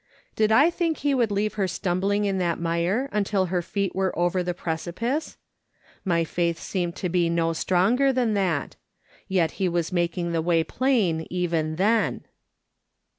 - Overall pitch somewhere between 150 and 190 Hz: Yes, medium, 185 Hz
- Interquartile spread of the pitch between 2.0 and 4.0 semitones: Yes, average, 3.7 semitones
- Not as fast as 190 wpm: Yes, average, 165 wpm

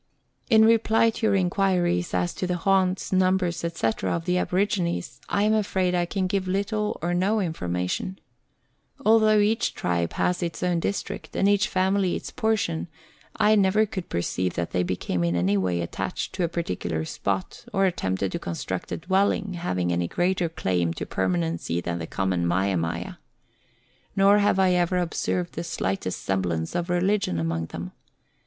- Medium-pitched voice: Yes, medium, 175 Hz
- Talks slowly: No, average, 170 wpm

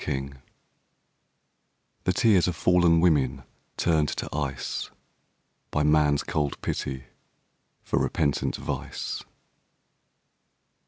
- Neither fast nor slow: No, slow, 90 wpm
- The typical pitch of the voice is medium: No, very low, 75 Hz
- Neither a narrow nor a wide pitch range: Yes, average, 3.4 semitones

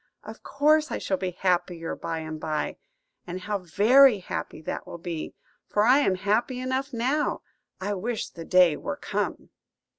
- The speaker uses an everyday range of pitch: No, wide, 6.4 semitones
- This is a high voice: Yes, high, 195 Hz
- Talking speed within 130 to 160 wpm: No, average, 170 wpm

